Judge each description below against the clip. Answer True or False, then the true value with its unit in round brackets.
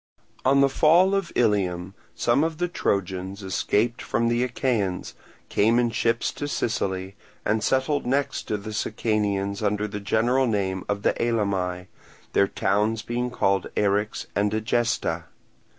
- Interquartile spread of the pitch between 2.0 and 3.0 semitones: False (3.6 semitones)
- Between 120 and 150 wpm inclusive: True (140 wpm)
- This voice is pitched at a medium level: False (110 Hz)